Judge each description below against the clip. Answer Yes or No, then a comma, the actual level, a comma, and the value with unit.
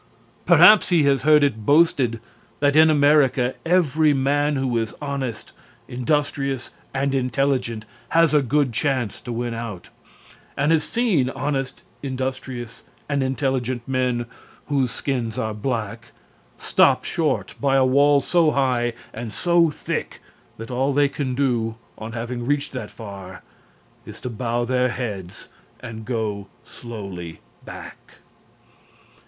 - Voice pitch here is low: Yes, low, 130 Hz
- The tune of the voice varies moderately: Yes, average, 3.5 semitones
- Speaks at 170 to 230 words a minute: No, slow, 135 wpm